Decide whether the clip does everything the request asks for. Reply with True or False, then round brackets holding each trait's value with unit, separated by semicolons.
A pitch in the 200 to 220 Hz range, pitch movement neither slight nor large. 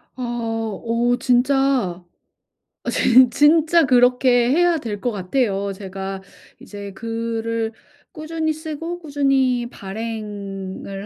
False (240 Hz; 4.9 semitones)